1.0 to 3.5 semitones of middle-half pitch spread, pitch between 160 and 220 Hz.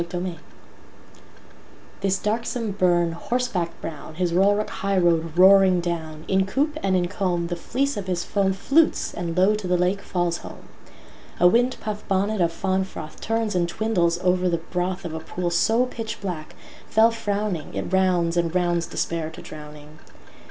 Yes: average, 3.0 semitones; medium, 185 Hz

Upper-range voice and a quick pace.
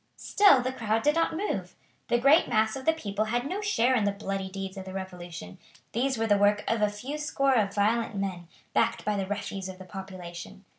Yes: high, 210 Hz; fast, 220 wpm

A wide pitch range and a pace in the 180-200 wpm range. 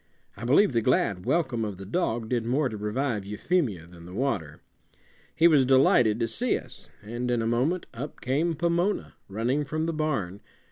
Yes: wide, 6.1 semitones; average, 185 wpm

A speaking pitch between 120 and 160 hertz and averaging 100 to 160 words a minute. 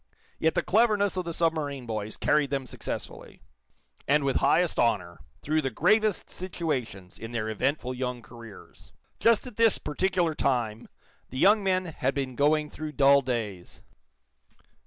Yes: medium, 140 Hz; average, 150 wpm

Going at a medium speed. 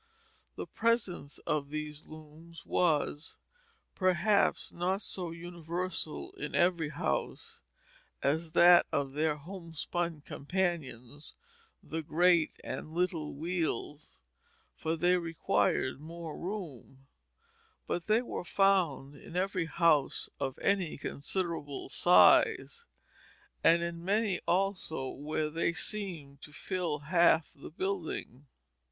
No: slow, 110 wpm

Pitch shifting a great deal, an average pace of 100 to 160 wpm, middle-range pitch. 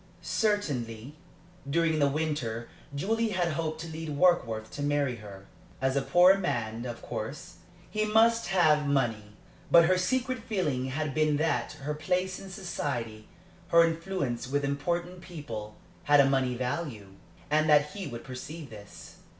Yes: wide, 5.7 semitones; average, 150 wpm; medium, 150 Hz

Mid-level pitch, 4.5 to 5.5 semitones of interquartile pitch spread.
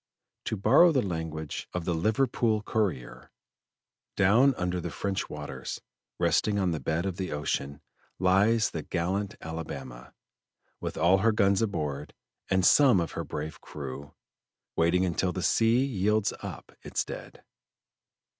No: very low, 95 Hz; average, 4.8 semitones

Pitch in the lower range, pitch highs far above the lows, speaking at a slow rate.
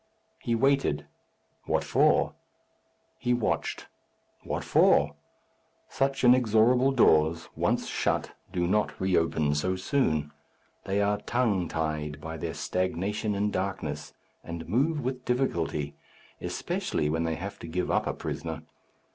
Yes: very low, 95 Hz; wide, 7.1 semitones; slow, 130 wpm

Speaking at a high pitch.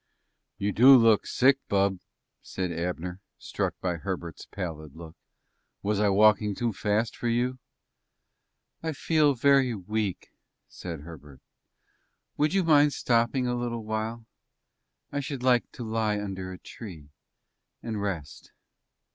No: low, 105 Hz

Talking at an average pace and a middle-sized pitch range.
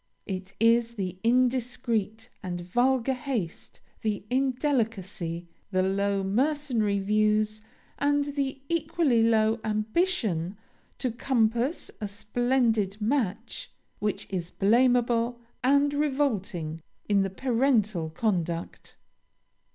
No: slow, 95 wpm; average, 4.5 semitones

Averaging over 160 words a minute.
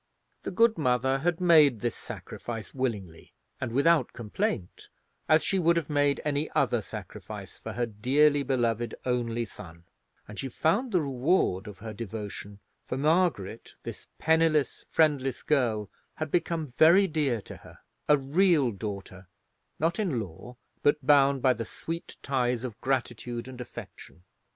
No: average, 145 wpm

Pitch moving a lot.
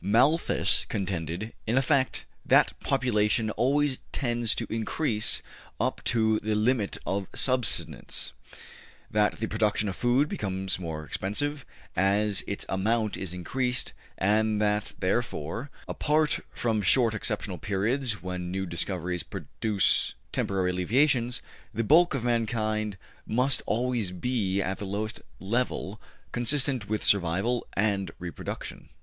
No: average, 4.1 semitones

